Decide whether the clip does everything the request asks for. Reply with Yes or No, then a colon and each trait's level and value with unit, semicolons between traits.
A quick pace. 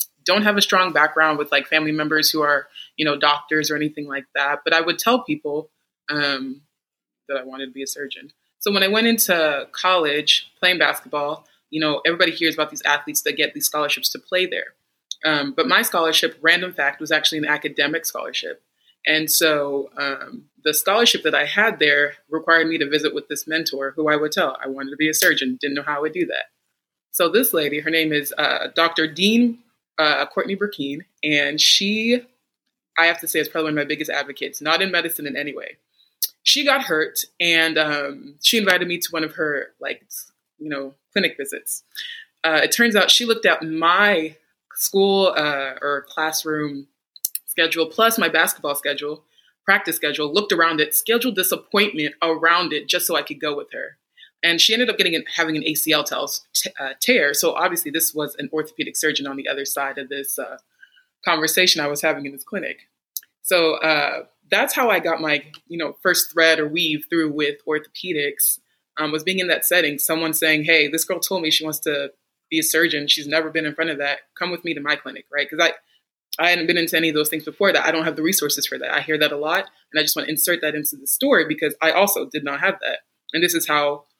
Yes: fast, 215 wpm